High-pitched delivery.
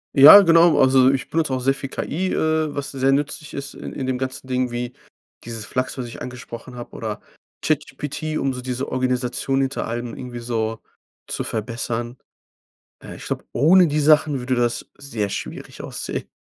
No: low, 130 Hz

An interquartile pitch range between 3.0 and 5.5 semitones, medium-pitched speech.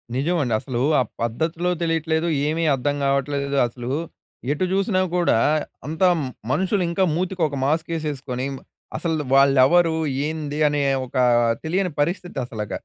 Yes: average, 3.8 semitones; medium, 155 Hz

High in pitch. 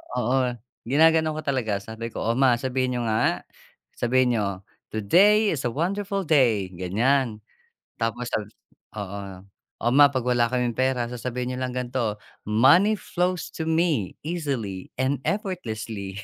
No: low, 125 Hz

